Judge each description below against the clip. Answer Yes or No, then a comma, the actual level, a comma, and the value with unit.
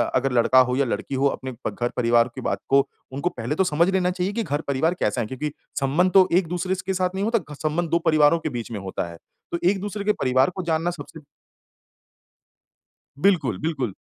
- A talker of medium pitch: Yes, medium, 155 Hz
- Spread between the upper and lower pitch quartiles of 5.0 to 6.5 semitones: Yes, wide, 5.5 semitones